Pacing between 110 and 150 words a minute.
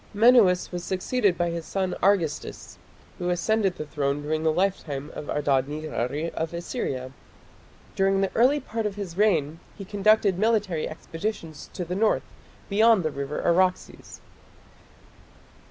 Yes: average, 140 wpm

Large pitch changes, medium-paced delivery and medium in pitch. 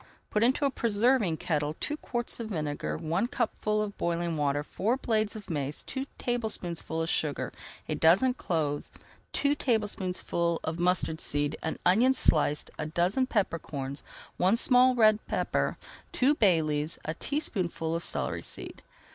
Yes: wide, 6.7 semitones; average, 165 wpm; medium, 180 Hz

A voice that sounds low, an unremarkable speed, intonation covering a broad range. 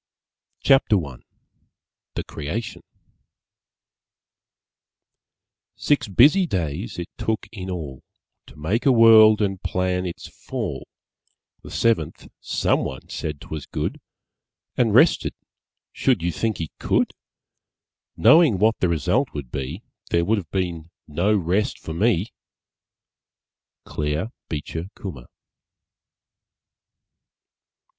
No: very low, 95 Hz; slow, 105 wpm; wide, 5.9 semitones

